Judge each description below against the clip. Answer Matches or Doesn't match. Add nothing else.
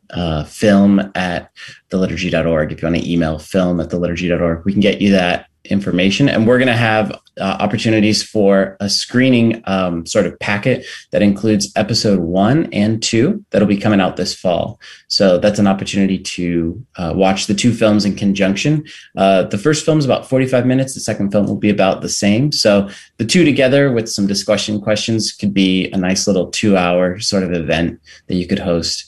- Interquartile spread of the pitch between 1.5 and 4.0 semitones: Matches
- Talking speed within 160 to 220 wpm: Matches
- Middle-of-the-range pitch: Doesn't match